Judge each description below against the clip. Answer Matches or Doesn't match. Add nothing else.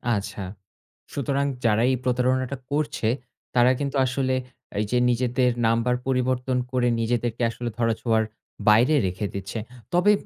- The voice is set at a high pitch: Doesn't match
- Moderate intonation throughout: Doesn't match